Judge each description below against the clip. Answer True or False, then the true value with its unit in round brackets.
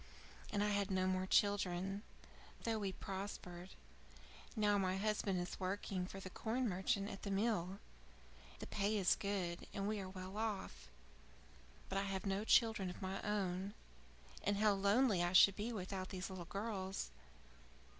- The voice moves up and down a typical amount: False (1.8 semitones)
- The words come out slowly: False (160 wpm)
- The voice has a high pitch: True (195 Hz)